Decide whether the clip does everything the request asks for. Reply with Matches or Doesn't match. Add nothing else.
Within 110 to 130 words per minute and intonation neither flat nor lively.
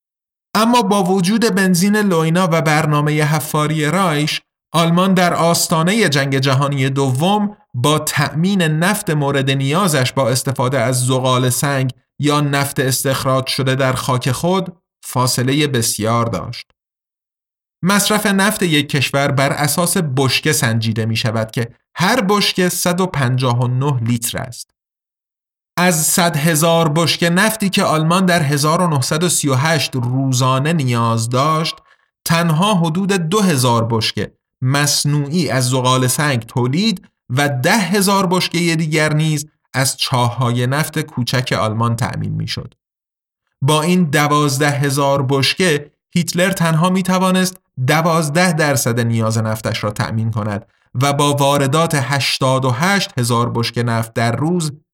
Matches